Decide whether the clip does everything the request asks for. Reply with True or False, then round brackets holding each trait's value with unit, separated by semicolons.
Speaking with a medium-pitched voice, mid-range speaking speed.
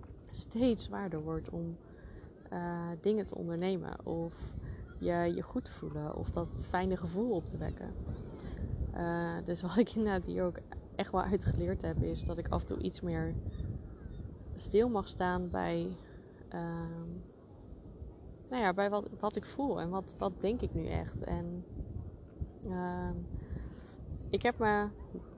True (170 Hz; 150 wpm)